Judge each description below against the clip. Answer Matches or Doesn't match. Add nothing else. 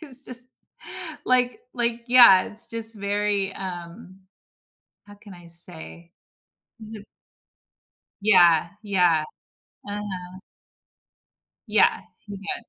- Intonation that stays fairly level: Doesn't match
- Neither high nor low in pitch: Doesn't match